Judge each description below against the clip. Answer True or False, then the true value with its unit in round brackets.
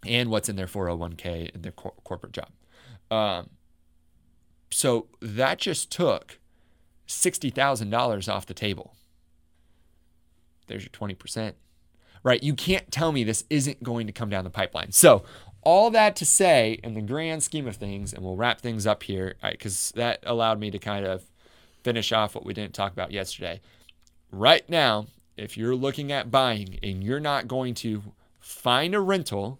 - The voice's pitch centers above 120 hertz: False (105 Hz)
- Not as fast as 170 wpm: False (175 wpm)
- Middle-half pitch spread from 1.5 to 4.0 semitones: False (5.1 semitones)